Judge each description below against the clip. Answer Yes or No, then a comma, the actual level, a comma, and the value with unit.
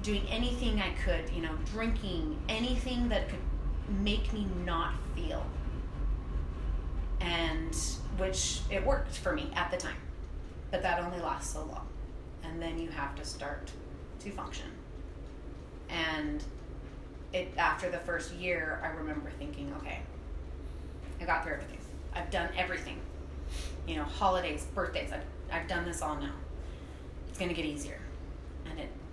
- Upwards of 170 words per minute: No, average, 145 wpm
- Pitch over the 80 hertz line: No, very low, 70 Hz